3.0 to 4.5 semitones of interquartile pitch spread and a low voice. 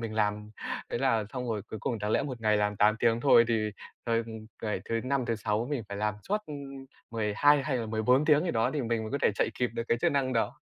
Yes: average, 3.3 semitones; low, 115 Hz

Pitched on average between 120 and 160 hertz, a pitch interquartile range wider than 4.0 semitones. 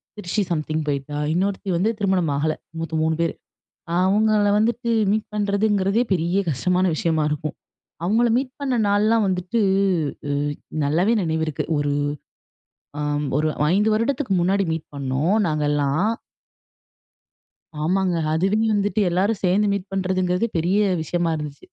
No: medium, 185 Hz; average, 4.6 semitones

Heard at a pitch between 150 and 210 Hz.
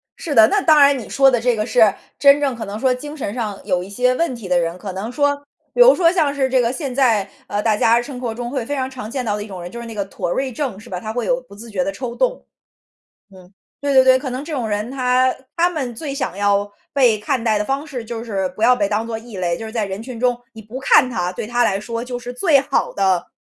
No: high, 240 Hz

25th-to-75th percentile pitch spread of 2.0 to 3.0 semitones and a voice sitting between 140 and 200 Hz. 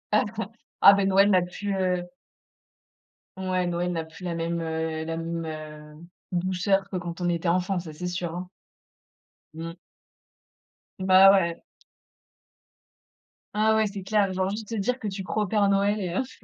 Yes: narrow, 2.6 semitones; medium, 185 Hz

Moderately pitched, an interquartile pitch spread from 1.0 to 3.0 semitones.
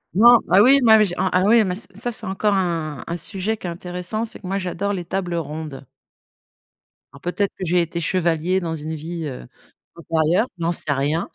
No: medium, 175 Hz; average, 3.4 semitones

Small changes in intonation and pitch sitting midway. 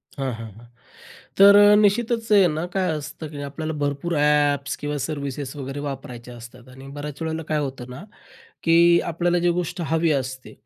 No: average, 3.6 semitones; medium, 145 Hz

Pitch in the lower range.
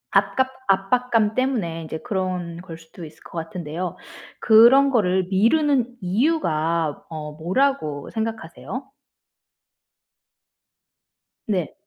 No: high, 190 Hz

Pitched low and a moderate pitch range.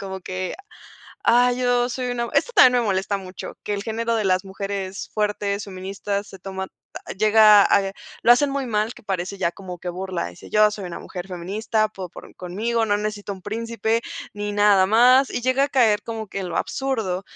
No: high, 205 Hz; average, 3.3 semitones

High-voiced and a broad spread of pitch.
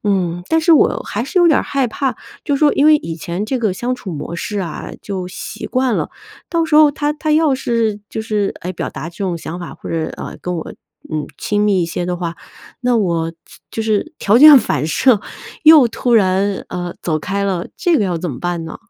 Yes: high, 205 Hz; wide, 7.1 semitones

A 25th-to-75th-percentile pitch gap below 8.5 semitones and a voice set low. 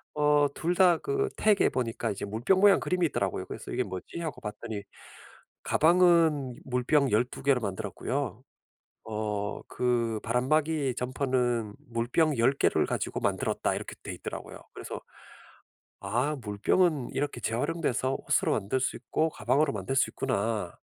Yes: average, 5.2 semitones; low, 130 Hz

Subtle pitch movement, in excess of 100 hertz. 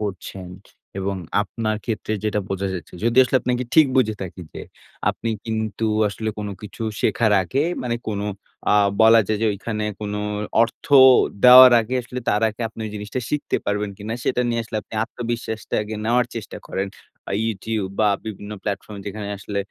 Yes: narrow, 2.2 semitones; low, 110 Hz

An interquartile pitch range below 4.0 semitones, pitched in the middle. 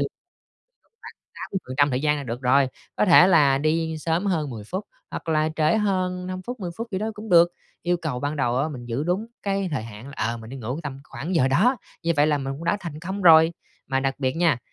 No: average, 5.1 semitones; medium, 155 Hz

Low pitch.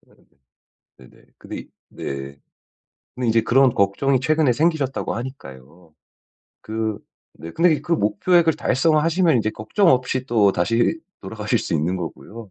Yes: low, 115 Hz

